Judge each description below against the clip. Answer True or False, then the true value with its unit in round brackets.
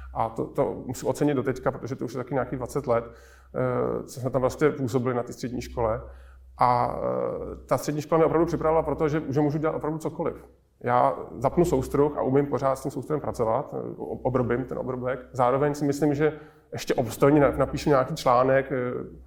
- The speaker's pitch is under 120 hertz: False (135 Hz)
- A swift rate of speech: True (195 wpm)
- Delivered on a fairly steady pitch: False (3.1 semitones)